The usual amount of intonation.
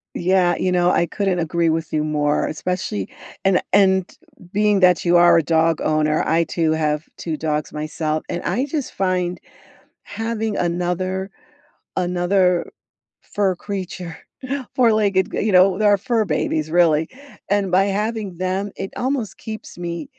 Yes: average, 3.3 semitones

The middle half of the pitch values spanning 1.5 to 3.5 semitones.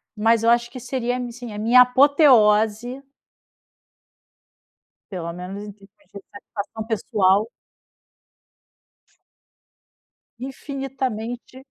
Yes: average, 3.2 semitones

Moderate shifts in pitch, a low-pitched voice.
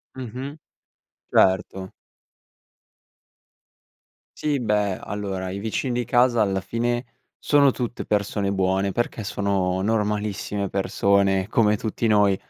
Yes: average, 3.3 semitones; low, 105 Hz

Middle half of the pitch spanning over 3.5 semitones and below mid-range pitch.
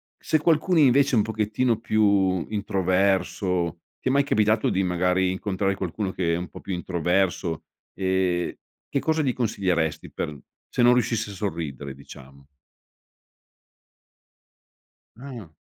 Yes: average, 3.9 semitones; very low, 95 Hz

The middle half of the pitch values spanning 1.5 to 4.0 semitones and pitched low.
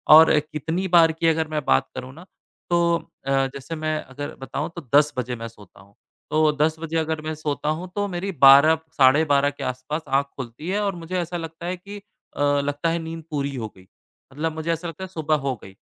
No: average, 3.1 semitones; medium, 155 Hz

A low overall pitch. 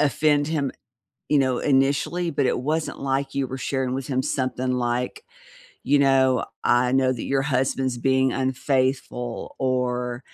Yes: low, 130 Hz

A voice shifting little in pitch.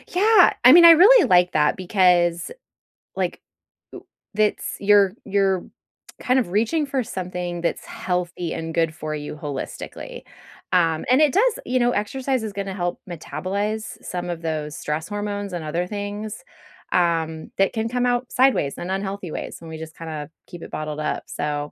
No: average, 5.0 semitones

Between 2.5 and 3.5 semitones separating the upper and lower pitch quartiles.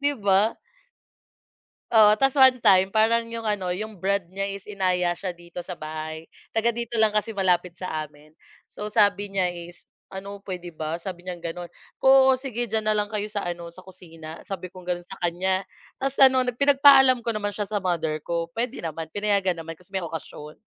No: average, 3.9 semitones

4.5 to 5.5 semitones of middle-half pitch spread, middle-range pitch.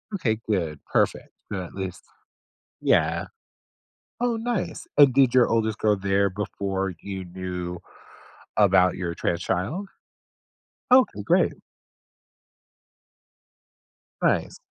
No: average, 4.8 semitones; very low, 95 Hz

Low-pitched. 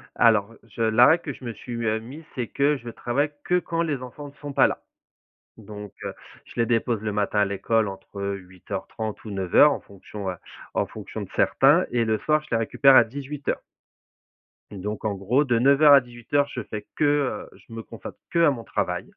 Yes: low, 115 Hz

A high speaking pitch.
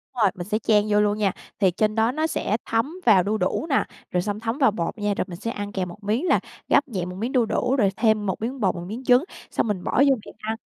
Yes: high, 215 Hz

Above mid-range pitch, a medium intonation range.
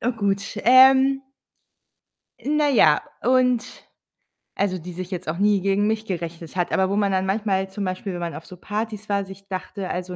Yes: high, 195 Hz; average, 3.1 semitones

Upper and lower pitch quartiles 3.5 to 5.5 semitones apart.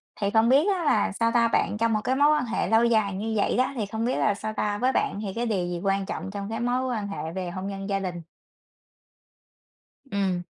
No: average, 3.1 semitones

